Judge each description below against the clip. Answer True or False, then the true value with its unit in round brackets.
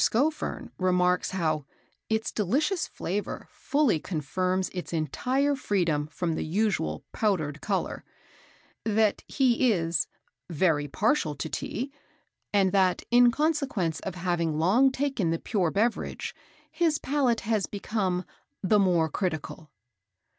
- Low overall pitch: False (190 Hz)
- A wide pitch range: True (6.2 semitones)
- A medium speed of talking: False (120 wpm)